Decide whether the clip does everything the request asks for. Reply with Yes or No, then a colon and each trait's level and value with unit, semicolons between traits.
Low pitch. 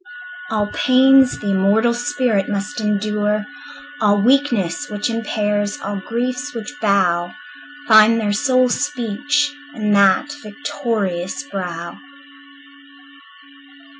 No: high, 215 Hz